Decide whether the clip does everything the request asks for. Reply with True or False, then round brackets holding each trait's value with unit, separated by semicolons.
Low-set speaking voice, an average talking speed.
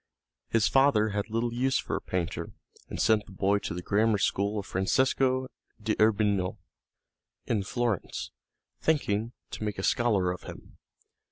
True (105 Hz; 150 wpm)